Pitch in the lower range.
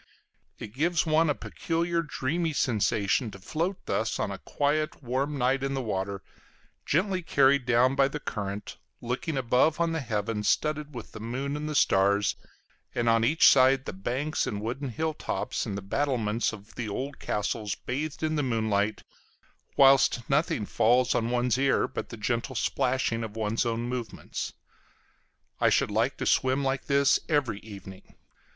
Yes: low, 125 Hz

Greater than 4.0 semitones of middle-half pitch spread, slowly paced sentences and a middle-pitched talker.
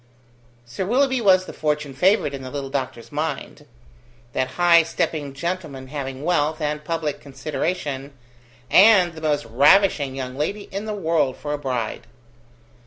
No: average, 4.5 semitones; average, 150 wpm; medium, 150 Hz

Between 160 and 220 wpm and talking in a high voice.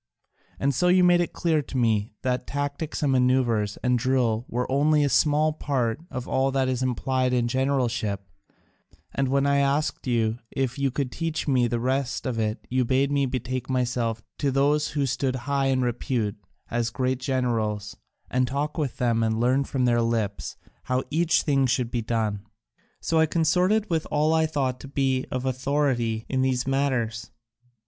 No: average, 180 wpm; low, 130 Hz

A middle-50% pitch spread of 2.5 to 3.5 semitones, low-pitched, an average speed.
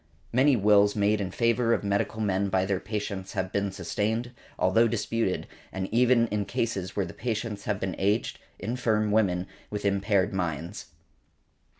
Yes: average, 2.9 semitones; low, 105 Hz; average, 165 wpm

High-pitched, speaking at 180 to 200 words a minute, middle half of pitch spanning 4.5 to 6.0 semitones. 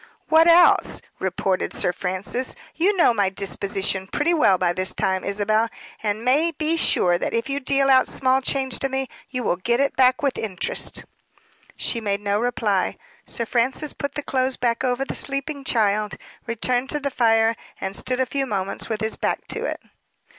Yes: high, 240 Hz; average, 190 wpm; average, 5.2 semitones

